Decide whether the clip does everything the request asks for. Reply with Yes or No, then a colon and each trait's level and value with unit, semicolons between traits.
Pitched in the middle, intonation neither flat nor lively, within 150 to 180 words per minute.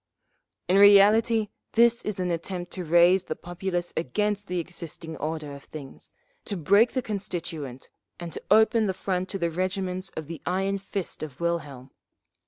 Yes: medium, 180 Hz; average, 3.3 semitones; average, 170 wpm